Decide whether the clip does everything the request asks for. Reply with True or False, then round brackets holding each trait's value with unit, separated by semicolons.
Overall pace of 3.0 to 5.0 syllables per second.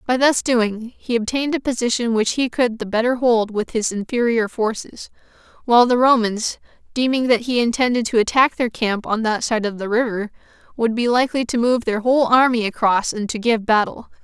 False (5.4 syllables/s)